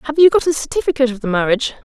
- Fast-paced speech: Yes, fast, 250 wpm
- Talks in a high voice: Yes, very high, 265 Hz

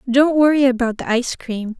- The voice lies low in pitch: No, very high, 255 Hz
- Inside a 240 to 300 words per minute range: No, average, 200 wpm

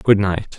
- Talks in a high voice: No, low, 100 Hz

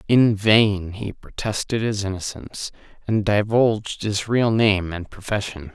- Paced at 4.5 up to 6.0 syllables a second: No, 4.2 syllables/s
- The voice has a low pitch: Yes, low, 105 Hz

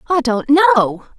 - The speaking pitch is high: Yes, very high, 280 Hz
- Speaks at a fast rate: No, average, 150 wpm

